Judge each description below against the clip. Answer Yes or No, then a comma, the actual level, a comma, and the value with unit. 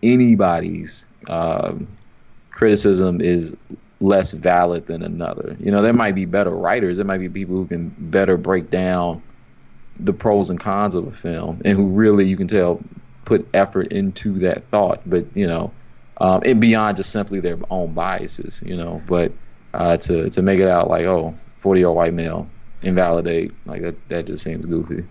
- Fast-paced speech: No, average, 180 wpm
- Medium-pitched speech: No, very low, 95 Hz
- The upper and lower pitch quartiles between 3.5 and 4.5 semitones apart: No, average, 2.7 semitones